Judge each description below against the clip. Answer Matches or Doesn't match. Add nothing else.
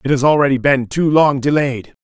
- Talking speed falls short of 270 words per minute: Matches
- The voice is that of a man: Matches